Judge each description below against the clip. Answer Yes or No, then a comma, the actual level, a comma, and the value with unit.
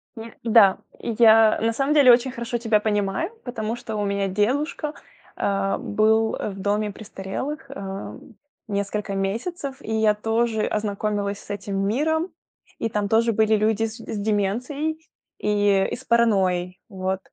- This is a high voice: Yes, high, 215 Hz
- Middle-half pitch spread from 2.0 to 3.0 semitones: Yes, narrow, 2.6 semitones